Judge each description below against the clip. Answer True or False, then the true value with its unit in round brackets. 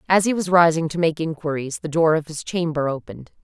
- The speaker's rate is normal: False (225 wpm)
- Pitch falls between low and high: True (160 Hz)